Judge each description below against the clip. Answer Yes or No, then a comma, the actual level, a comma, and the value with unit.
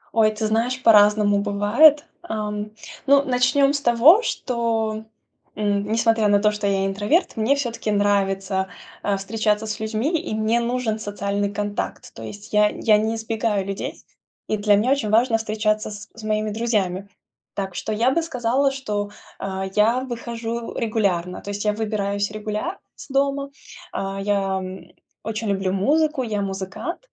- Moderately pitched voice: No, high, 215 Hz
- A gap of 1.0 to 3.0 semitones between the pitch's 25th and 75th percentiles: Yes, narrow, 2.6 semitones